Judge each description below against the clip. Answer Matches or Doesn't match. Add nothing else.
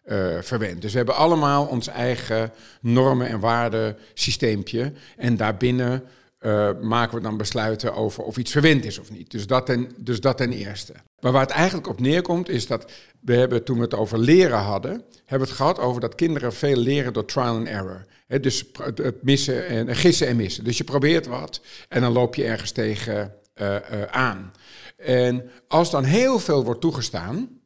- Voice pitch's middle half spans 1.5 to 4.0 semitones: Matches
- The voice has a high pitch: Doesn't match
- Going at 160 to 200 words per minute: Matches